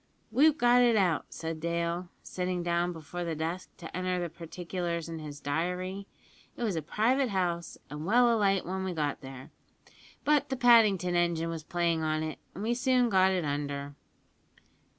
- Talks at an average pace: Yes, average, 175 wpm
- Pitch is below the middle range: No, medium, 175 Hz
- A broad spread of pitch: No, average, 3.5 semitones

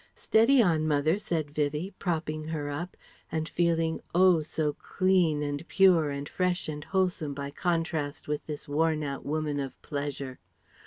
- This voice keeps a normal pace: Yes, average, 155 wpm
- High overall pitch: No, medium, 155 Hz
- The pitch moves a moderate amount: Yes, average, 3.2 semitones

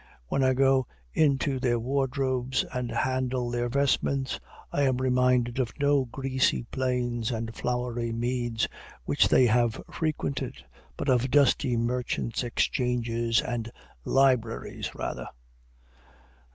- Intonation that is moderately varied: No, narrow, 1.8 semitones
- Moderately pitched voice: No, low, 125 Hz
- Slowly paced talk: Yes, slow, 115 wpm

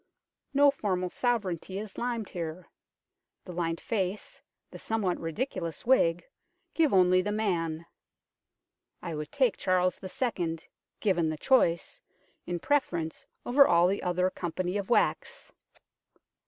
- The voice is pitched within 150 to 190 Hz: Yes, medium, 185 Hz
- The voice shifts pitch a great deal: No, average, 4.4 semitones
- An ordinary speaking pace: No, slow, 125 wpm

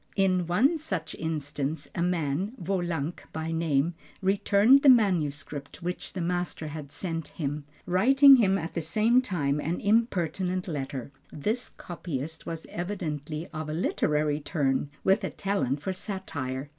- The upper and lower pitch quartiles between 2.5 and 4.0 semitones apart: No, average, 4.4 semitones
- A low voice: No, medium, 170 Hz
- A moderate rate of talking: Yes, average, 145 wpm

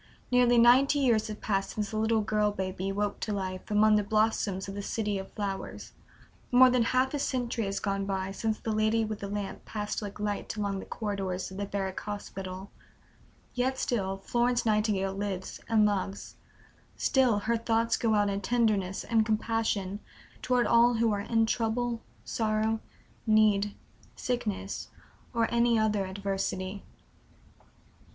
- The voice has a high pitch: Yes, high, 210 Hz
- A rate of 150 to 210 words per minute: Yes, average, 160 wpm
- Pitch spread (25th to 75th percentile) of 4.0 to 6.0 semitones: No, narrow, 2.5 semitones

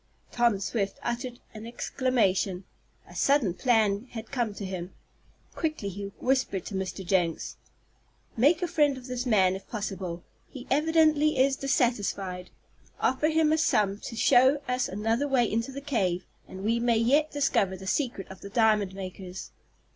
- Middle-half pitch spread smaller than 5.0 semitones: No, wide, 5.5 semitones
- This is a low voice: No, high, 230 Hz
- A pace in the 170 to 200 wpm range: No, average, 160 wpm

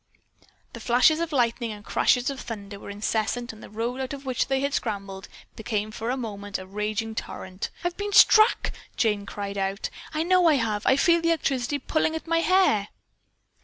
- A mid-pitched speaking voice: No, high, 235 Hz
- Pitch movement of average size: No, wide, 5.8 semitones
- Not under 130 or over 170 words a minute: No, average, 195 wpm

